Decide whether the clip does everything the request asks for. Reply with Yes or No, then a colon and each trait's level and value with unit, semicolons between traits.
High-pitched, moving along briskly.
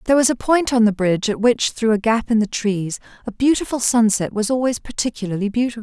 Yes: high, 225 Hz; fast, 225 wpm